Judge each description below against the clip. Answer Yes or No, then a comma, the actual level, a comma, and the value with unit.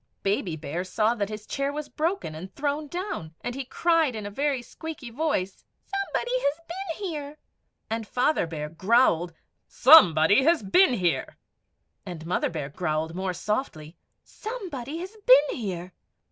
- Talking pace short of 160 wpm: Yes, average, 150 wpm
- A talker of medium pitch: No, high, 235 Hz